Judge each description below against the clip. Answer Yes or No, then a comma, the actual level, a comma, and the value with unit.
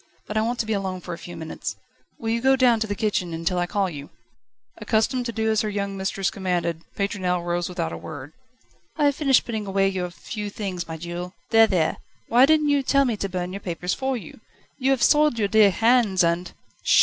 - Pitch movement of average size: Yes, average, 4.5 semitones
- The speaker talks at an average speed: No, fast, 225 wpm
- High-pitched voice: Yes, high, 200 Hz